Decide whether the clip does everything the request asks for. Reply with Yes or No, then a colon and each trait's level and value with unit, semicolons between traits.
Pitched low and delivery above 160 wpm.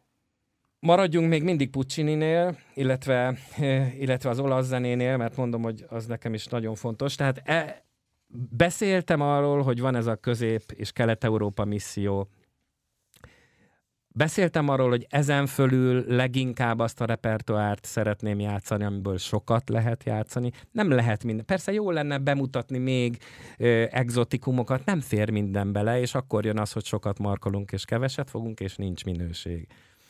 No: low, 120 Hz; average, 140 wpm